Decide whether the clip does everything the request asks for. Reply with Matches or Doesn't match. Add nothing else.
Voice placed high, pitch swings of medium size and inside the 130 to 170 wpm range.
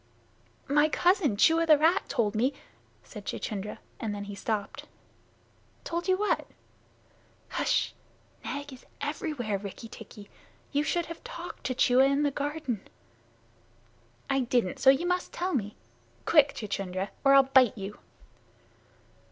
Doesn't match